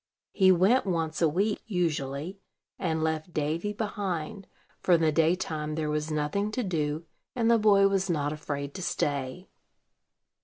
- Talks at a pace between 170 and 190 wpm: No, average, 155 wpm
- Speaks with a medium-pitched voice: Yes, medium, 165 Hz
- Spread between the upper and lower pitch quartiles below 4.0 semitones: No, average, 4.4 semitones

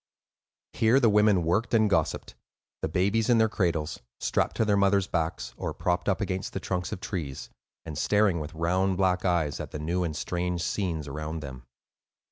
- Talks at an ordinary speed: Yes, average, 180 wpm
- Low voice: Yes, very low, 90 Hz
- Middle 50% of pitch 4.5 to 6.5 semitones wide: No, average, 4.0 semitones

